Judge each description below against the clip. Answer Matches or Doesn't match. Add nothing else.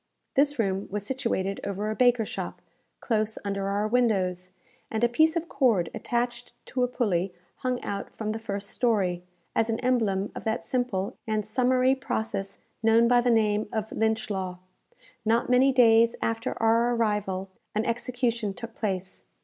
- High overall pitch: Matches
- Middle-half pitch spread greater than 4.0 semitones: Doesn't match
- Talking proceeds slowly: Doesn't match